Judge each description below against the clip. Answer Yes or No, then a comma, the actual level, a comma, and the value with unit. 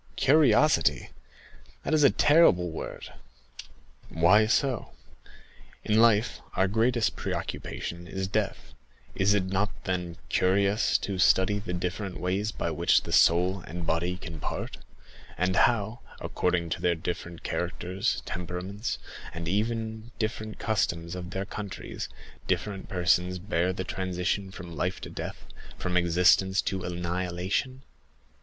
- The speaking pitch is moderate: No, very low, 95 Hz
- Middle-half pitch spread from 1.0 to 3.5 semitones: Yes, average, 3.1 semitones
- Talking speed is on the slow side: Yes, slow, 130 wpm